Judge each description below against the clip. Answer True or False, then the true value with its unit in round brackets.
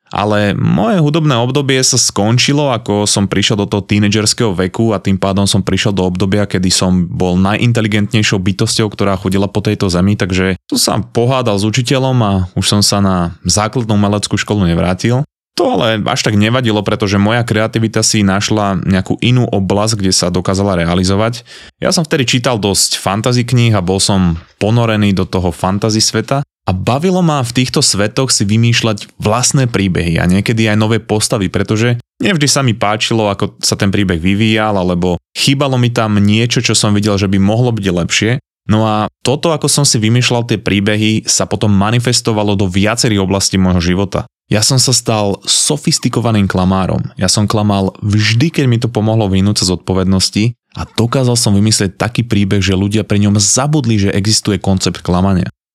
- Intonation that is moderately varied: True (3.3 semitones)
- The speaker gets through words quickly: True (180 wpm)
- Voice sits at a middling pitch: False (105 Hz)